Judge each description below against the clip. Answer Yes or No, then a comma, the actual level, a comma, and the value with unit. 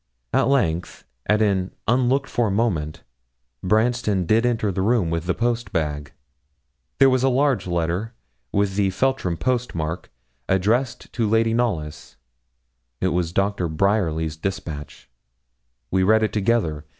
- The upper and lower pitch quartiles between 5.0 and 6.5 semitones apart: Yes, wide, 5.5 semitones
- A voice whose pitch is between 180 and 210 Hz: No, low, 100 Hz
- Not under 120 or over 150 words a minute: Yes, average, 140 wpm